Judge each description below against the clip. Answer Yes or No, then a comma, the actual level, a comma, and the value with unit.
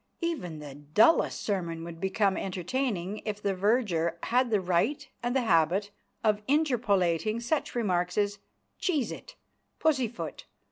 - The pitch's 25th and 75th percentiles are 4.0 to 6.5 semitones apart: Yes, wide, 5.5 semitones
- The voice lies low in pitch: No, high, 205 Hz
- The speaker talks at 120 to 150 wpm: Yes, slow, 135 wpm